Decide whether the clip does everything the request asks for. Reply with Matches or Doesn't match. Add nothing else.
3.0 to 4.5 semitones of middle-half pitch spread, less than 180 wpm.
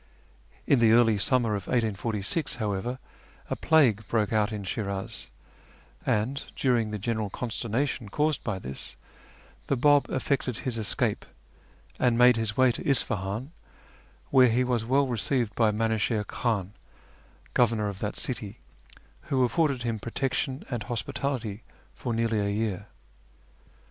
Matches